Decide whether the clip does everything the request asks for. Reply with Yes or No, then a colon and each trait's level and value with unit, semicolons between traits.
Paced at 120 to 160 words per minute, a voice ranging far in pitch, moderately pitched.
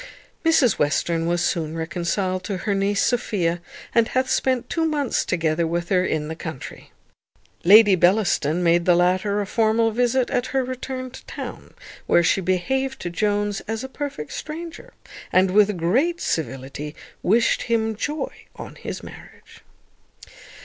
No: average, 150 wpm; wide, 6.3 semitones; high, 200 Hz